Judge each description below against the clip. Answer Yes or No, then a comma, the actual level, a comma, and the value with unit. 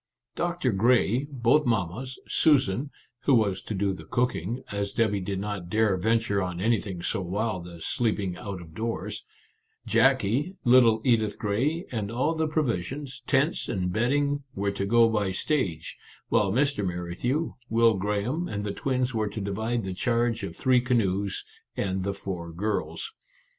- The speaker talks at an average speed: Yes, average, 160 wpm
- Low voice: Yes, low, 110 Hz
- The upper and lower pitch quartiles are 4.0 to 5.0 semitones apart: Yes, average, 4.6 semitones